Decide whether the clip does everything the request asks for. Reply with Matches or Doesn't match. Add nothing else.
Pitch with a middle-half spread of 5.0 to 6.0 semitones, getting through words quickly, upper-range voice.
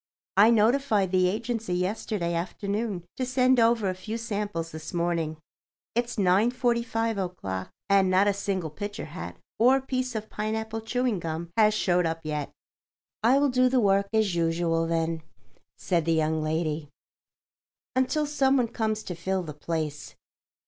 Doesn't match